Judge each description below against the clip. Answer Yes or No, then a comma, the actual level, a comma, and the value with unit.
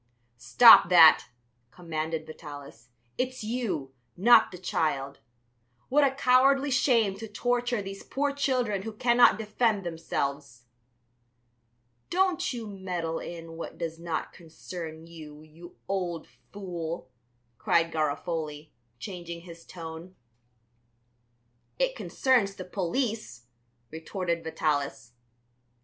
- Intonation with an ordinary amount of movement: No, wide, 5.9 semitones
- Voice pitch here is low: No, medium, 175 Hz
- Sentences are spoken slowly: Yes, slow, 105 wpm